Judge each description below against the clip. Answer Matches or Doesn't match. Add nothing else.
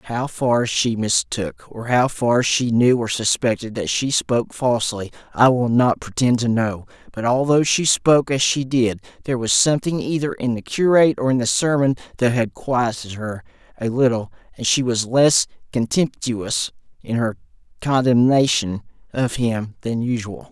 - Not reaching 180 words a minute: Matches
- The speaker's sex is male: Matches